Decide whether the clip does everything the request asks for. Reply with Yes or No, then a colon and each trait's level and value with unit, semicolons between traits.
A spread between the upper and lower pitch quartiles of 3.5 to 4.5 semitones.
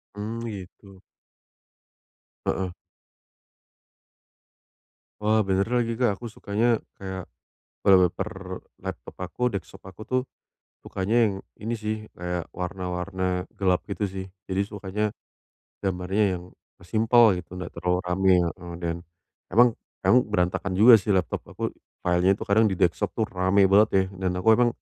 No: average, 3.0 semitones